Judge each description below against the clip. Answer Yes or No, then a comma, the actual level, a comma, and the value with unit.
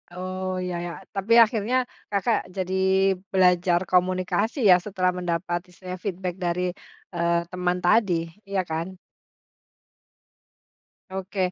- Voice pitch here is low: No, medium, 185 Hz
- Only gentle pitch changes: Yes, narrow, 1.4 semitones